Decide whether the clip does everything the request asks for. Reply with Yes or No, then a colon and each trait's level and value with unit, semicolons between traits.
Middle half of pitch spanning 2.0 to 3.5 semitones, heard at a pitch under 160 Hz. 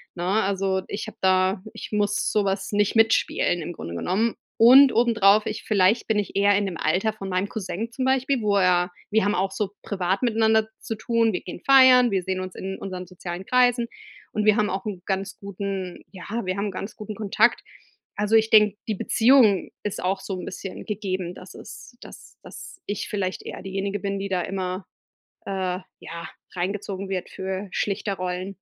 No: narrow, 2.5 semitones; high, 200 Hz